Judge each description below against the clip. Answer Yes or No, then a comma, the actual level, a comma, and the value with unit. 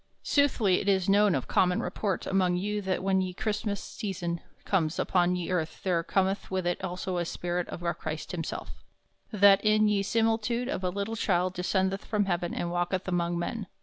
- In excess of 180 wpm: Yes, average, 190 wpm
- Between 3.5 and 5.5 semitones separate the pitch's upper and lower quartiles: No, narrow, 2.5 semitones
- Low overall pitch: No, high, 190 Hz